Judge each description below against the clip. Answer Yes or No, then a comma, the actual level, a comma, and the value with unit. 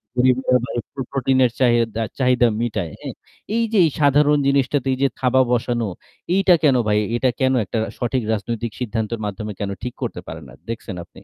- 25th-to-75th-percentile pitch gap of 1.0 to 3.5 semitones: Yes, average, 2.9 semitones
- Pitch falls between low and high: No, low, 125 Hz